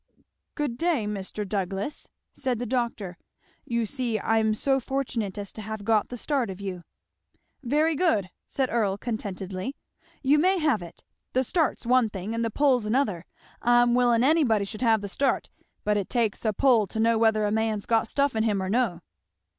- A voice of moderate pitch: No, high, 225 Hz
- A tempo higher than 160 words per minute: Yes, average, 185 wpm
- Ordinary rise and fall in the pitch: Yes, average, 3.9 semitones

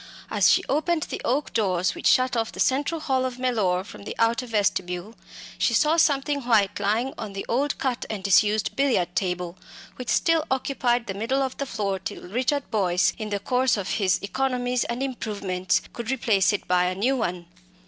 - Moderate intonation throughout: Yes, average, 5.0 semitones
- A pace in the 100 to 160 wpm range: No, average, 190 wpm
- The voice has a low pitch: No, high, 230 Hz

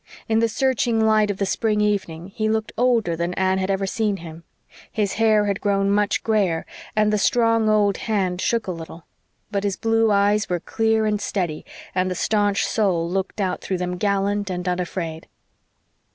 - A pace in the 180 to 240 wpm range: Yes, average, 185 wpm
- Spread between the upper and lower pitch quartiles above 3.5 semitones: No, average, 2.9 semitones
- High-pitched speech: Yes, high, 200 Hz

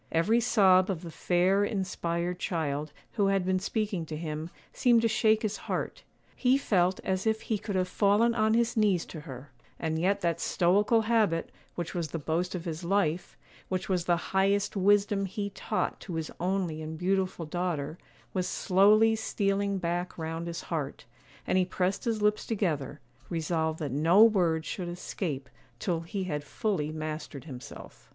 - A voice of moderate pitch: Yes, medium, 180 Hz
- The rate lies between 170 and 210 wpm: Yes, average, 175 wpm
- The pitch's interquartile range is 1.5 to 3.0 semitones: No, average, 3.7 semitones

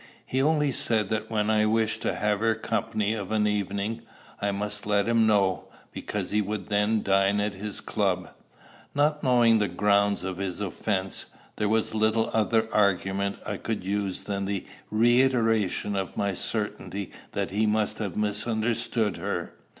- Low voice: Yes, low, 105 Hz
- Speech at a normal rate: Yes, average, 165 wpm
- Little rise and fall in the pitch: Yes, narrow, 1.8 semitones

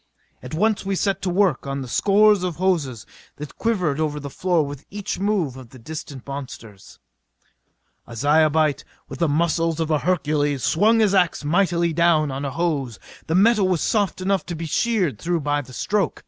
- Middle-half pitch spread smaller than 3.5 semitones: No, average, 4.7 semitones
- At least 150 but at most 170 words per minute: No, average, 190 wpm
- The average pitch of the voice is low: No, medium, 165 Hz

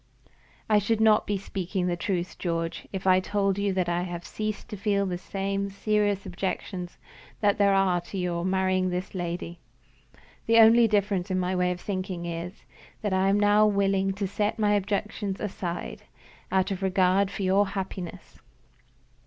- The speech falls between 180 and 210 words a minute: No, average, 170 wpm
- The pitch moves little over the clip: Yes, narrow, 2.1 semitones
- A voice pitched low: No, high, 195 Hz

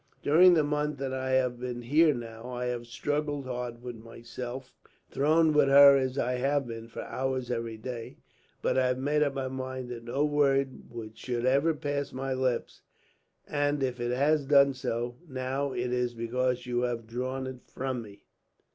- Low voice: Yes, low, 130 Hz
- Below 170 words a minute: No, average, 180 wpm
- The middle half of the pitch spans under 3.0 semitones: Yes, narrow, 2.4 semitones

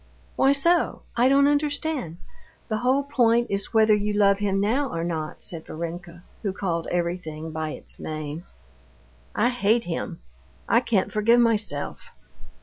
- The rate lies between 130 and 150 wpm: Yes, average, 145 wpm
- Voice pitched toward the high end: Yes, high, 205 Hz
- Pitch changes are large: Yes, wide, 6.2 semitones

